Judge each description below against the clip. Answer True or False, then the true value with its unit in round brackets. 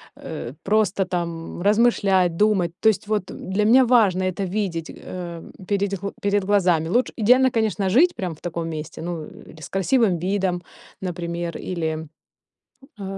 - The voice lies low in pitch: False (190 Hz)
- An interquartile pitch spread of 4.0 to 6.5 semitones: False (3.6 semitones)